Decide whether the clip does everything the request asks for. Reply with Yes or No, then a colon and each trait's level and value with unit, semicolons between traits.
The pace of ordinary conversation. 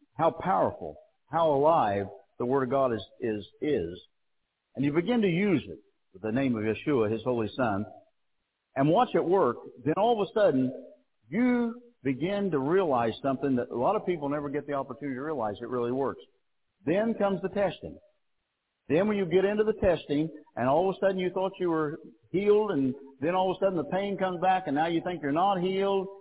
No: fast, 210 wpm